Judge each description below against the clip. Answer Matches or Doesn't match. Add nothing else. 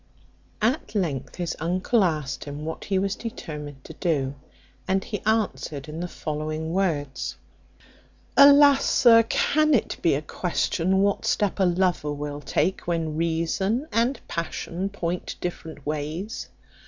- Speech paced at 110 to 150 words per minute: Matches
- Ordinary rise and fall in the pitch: Matches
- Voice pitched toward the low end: Doesn't match